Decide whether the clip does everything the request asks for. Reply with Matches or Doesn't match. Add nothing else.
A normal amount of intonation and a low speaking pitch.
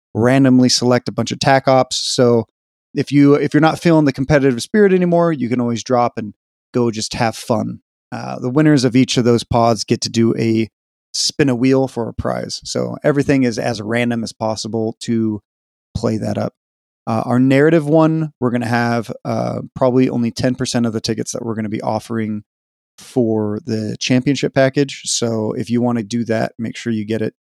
Matches